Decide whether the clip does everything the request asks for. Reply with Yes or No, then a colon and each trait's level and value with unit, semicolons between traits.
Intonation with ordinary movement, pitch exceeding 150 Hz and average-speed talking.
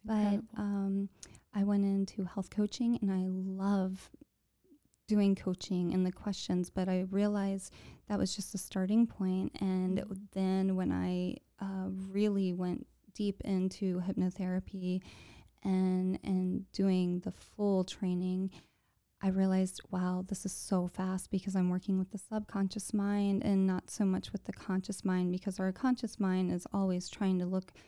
No: narrow, 1.4 semitones; high, 190 Hz; average, 155 wpm